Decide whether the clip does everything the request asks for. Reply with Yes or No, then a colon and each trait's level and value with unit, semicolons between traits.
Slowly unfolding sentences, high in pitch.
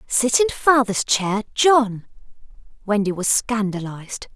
Yes: slow, 110 wpm; high, 220 Hz